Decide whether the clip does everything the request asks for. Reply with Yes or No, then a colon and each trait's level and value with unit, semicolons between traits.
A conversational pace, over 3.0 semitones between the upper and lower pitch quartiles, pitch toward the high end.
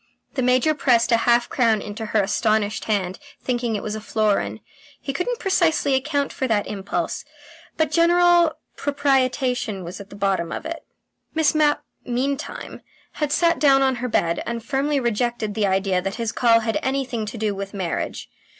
Yes: average, 175 wpm; average, 5.1 semitones; high, 240 Hz